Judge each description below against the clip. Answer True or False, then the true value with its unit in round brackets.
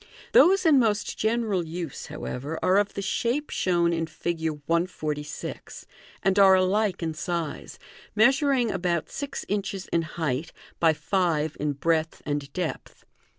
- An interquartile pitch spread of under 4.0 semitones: False (4.4 semitones)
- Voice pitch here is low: False (175 Hz)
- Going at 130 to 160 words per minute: True (140 wpm)